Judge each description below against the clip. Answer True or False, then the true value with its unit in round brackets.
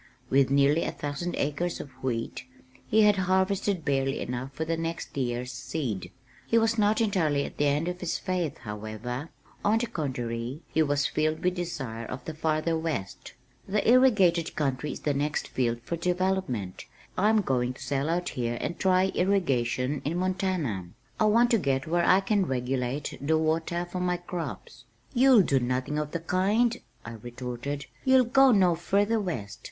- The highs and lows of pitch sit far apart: True (6.0 semitones)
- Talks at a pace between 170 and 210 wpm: True (175 wpm)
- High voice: False (160 Hz)